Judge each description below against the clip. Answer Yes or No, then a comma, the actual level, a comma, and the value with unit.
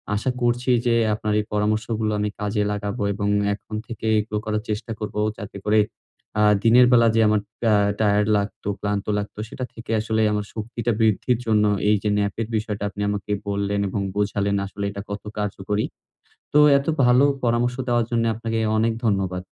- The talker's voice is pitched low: Yes, low, 105 Hz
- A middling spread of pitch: No, narrow, 1.9 semitones